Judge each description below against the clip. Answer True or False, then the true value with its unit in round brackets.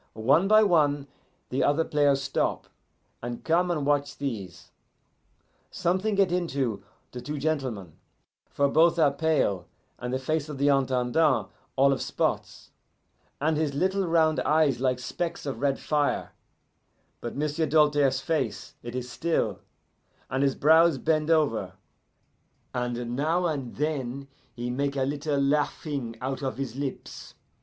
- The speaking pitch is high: False (140 Hz)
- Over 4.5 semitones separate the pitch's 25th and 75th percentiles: False (3.5 semitones)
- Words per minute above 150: False (145 wpm)